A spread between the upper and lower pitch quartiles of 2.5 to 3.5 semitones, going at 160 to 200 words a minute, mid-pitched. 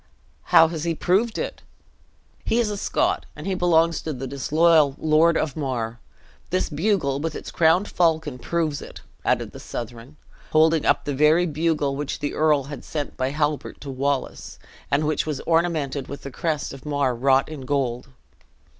Yes: average, 3.0 semitones; average, 175 wpm; medium, 150 Hz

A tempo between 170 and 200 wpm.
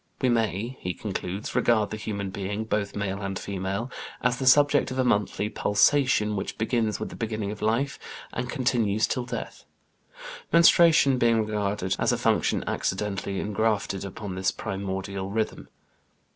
No: average, 155 wpm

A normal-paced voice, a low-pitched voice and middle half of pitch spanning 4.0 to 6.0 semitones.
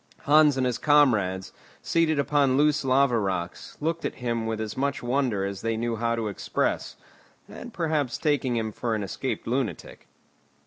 Yes: average, 170 wpm; low, 125 Hz; average, 4.5 semitones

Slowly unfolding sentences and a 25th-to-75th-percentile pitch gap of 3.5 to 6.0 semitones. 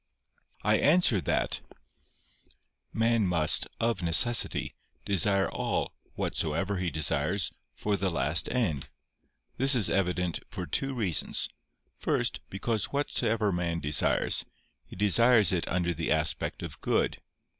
Yes: slow, 120 wpm; average, 5.1 semitones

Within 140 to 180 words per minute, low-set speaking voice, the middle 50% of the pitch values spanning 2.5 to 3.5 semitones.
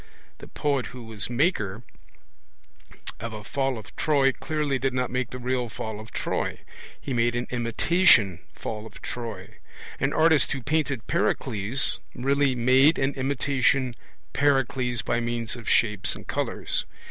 Yes: average, 145 wpm; low, 125 Hz; average, 2.9 semitones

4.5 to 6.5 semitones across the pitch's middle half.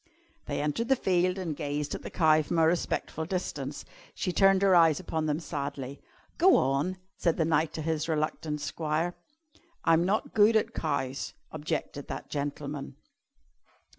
No: average, 3.2 semitones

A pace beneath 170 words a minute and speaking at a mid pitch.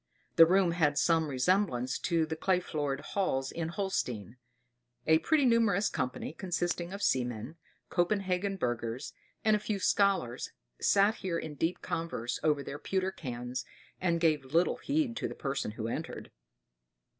Yes: average, 150 wpm; medium, 165 Hz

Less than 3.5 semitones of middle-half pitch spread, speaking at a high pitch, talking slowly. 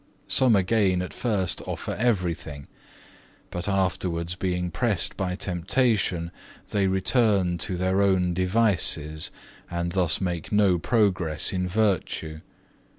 No: narrow, 2.6 semitones; very low, 95 Hz; slow, 115 wpm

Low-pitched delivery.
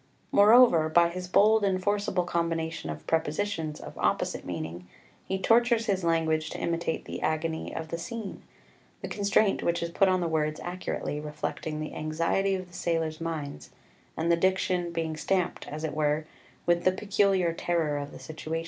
No: medium, 170 Hz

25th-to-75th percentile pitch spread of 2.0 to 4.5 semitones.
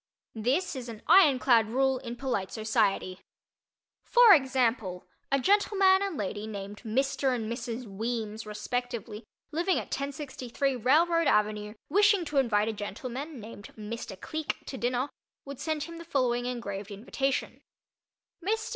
No: average, 5.1 semitones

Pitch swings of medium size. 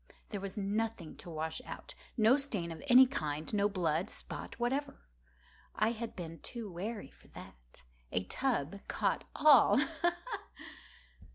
No: wide, 6.5 semitones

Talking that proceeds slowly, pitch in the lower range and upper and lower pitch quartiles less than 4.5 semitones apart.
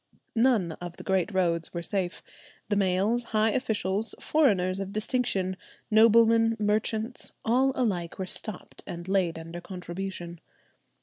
No: slow, 130 wpm; high, 195 Hz; average, 3.9 semitones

